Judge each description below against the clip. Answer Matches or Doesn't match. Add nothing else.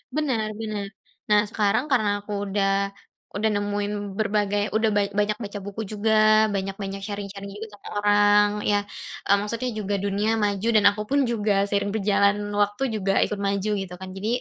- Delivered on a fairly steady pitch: Matches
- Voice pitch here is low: Doesn't match